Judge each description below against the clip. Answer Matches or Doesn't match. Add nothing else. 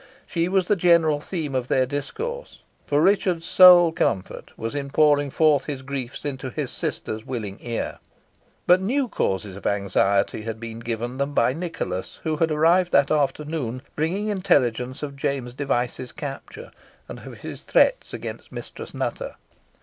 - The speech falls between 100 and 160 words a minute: Matches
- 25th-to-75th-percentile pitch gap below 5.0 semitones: Doesn't match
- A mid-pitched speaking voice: Matches